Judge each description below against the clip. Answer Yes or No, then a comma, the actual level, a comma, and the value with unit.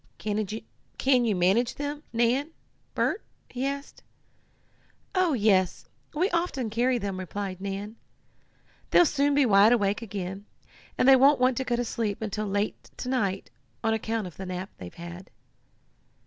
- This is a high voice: Yes, high, 225 Hz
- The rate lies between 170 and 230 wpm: No, average, 150 wpm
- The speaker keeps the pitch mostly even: No, average, 4.8 semitones